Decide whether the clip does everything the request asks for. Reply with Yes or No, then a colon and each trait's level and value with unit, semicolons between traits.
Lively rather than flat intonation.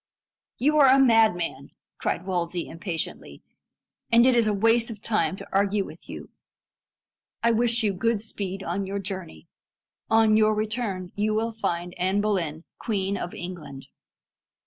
No: average, 3.9 semitones